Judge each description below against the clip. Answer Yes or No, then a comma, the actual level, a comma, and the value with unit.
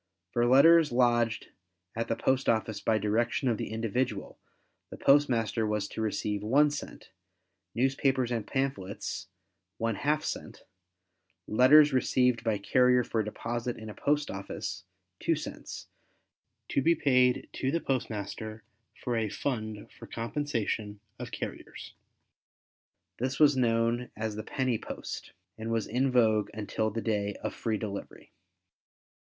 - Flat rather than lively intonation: No, average, 3.2 semitones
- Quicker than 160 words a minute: No, slow, 135 wpm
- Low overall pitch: Yes, low, 115 Hz